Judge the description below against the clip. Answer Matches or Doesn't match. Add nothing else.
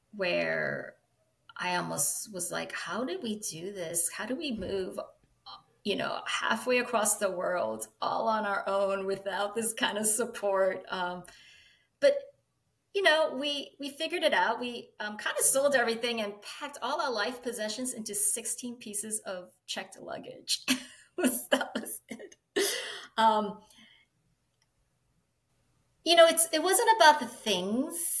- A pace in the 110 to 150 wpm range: Matches